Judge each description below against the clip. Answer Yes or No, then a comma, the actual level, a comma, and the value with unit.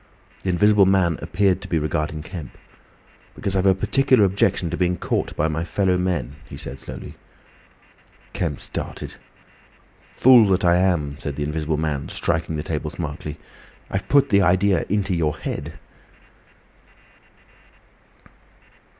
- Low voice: Yes, very low, 85 Hz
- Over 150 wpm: No, average, 140 wpm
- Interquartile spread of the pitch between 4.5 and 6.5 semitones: No, average, 3.9 semitones